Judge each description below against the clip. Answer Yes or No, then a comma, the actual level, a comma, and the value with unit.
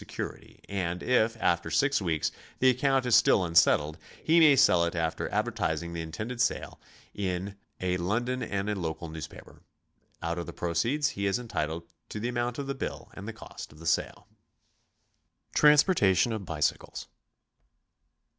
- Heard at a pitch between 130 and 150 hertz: No, low, 100 Hz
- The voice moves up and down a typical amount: No, wide, 6.5 semitones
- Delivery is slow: No, average, 165 wpm